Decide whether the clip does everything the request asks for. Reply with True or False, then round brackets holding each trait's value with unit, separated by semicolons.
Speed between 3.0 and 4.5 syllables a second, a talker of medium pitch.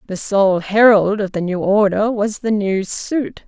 False (4.0 syllables/s; 205 Hz)